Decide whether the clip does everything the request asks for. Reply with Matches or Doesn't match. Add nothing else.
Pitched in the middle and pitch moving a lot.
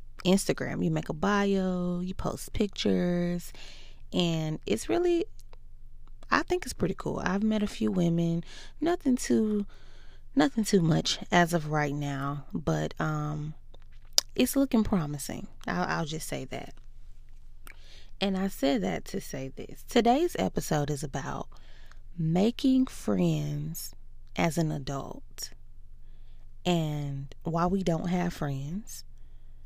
Matches